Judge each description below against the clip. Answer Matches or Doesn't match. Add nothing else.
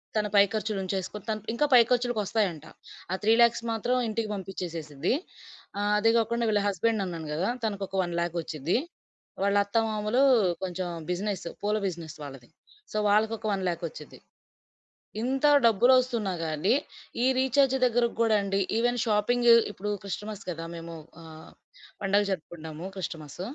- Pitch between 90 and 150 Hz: Doesn't match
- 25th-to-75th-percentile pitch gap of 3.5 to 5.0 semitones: Matches